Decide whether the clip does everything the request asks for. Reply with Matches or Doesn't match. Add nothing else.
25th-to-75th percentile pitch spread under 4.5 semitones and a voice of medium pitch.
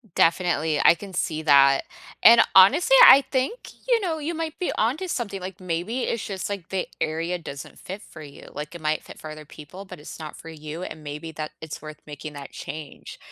Doesn't match